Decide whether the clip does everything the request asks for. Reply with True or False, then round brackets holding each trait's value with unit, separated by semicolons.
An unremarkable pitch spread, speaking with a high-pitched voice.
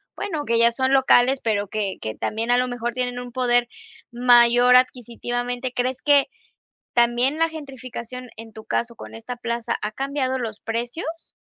False (1.6 semitones; 245 Hz)